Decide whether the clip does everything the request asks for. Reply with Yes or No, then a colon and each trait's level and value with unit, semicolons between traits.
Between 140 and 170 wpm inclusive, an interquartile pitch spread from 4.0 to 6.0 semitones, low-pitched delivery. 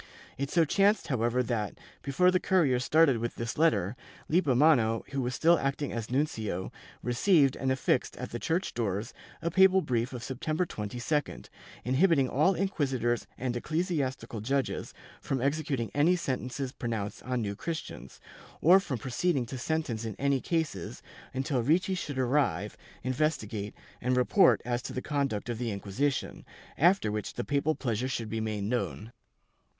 Yes: average, 160 wpm; average, 5.0 semitones; low, 130 Hz